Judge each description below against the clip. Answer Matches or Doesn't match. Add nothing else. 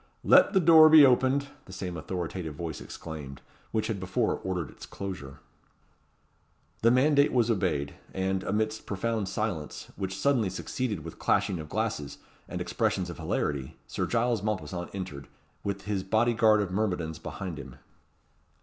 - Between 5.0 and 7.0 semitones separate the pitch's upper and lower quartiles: Doesn't match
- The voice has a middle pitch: Doesn't match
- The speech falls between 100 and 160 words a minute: Matches